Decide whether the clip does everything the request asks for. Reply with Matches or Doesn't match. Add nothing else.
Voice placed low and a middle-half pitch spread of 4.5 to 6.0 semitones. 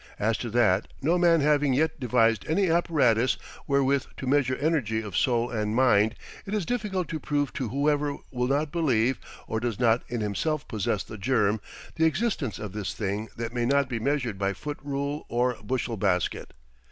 Matches